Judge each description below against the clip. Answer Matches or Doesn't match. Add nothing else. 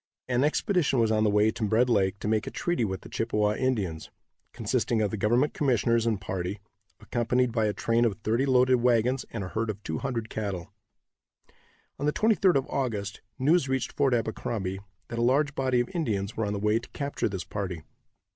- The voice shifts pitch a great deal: Doesn't match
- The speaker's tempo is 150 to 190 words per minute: Doesn't match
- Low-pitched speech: Matches